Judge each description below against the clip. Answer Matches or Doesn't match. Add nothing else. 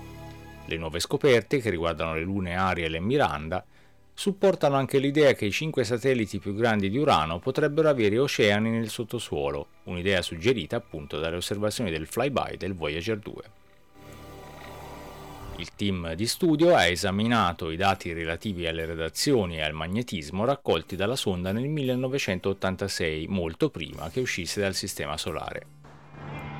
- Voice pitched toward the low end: Matches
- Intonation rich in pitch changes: Matches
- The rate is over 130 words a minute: Matches